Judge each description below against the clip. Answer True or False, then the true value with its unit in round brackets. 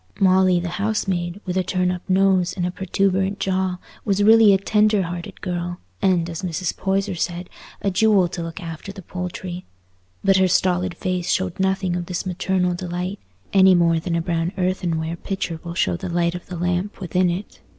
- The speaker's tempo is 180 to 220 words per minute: True (190 wpm)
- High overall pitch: False (180 Hz)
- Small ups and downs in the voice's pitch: True (1.7 semitones)